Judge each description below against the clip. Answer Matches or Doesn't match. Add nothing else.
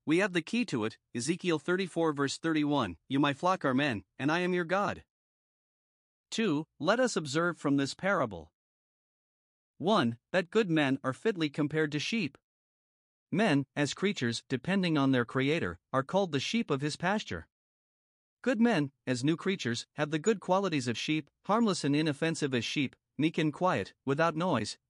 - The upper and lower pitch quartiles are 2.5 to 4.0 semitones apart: Doesn't match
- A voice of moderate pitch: Matches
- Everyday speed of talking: Matches